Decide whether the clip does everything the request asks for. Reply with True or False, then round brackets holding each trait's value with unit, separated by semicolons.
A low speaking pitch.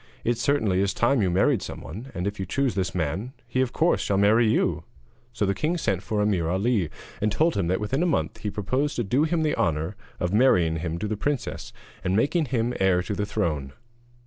True (105 Hz)